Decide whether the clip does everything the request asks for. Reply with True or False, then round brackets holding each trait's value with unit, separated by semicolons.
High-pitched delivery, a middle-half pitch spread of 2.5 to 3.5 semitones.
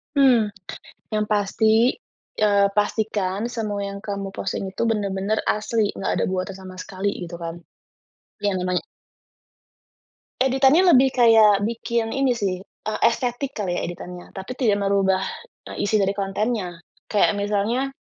True (205 Hz; 2.9 semitones)